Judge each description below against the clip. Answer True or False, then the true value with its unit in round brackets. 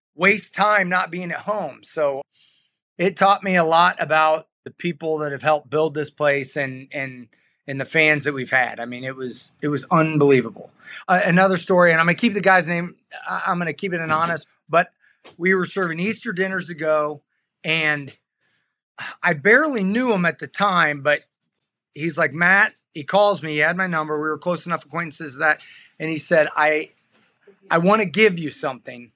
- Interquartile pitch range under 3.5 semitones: False (3.8 semitones)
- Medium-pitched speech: True (160 Hz)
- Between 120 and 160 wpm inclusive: False (195 wpm)